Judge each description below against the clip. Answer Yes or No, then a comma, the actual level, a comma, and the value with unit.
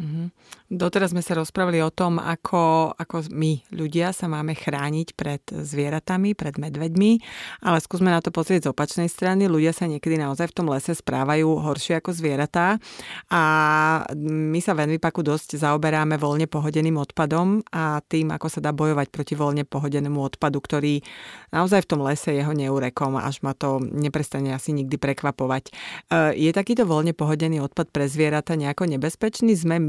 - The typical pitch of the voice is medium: Yes, medium, 155 Hz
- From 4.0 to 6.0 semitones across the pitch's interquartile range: No, narrow, 2.5 semitones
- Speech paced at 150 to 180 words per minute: Yes, fast, 165 wpm